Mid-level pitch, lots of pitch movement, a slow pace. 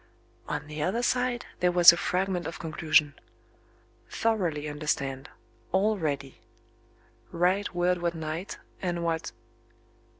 No: medium, 170 Hz; average, 3.4 semitones; slow, 125 wpm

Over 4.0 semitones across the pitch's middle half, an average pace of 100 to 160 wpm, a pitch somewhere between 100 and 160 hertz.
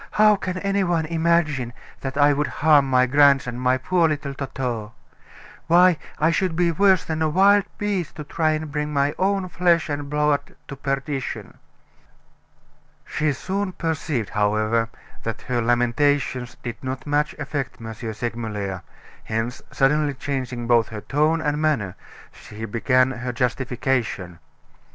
Yes: average, 4.7 semitones; average, 145 wpm; medium, 140 Hz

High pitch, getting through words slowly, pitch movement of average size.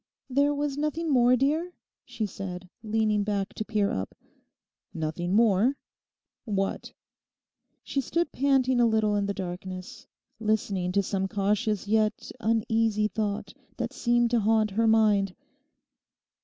Yes: high, 215 Hz; slow, 130 wpm; average, 3.2 semitones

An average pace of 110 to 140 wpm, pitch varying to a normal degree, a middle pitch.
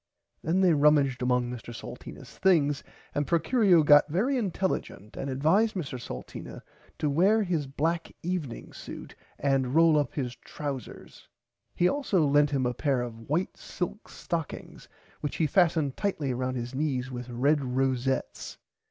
No: average, 150 wpm; average, 4.7 semitones; medium, 145 Hz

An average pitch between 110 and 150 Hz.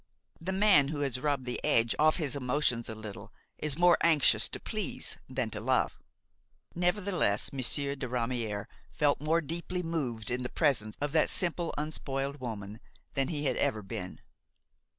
Yes: medium, 140 Hz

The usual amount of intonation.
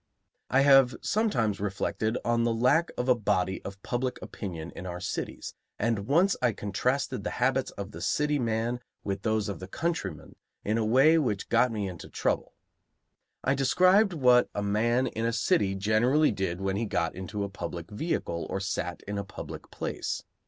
Yes: average, 4.6 semitones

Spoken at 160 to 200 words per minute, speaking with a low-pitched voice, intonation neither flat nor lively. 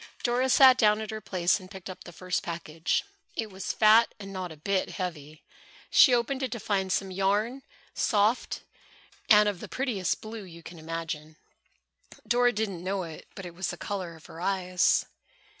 No: average, 185 wpm; high, 195 Hz; average, 3.8 semitones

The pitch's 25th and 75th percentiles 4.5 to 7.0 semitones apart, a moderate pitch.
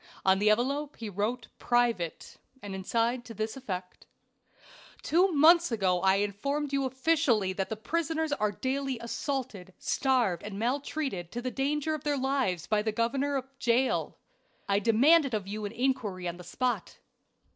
No: average, 5.2 semitones; high, 240 Hz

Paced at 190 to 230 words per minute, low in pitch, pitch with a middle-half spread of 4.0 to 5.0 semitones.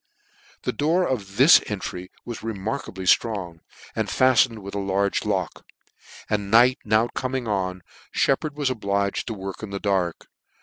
No: average, 160 wpm; low, 105 Hz; average, 4.6 semitones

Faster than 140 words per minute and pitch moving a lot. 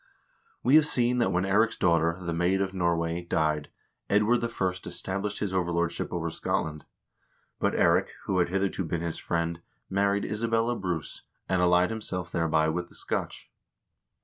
No: average, 155 wpm; average, 3.1 semitones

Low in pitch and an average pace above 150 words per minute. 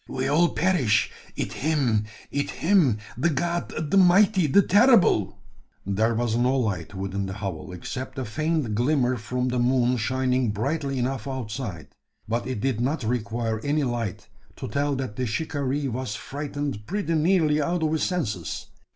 Yes: low, 130 Hz; average, 165 wpm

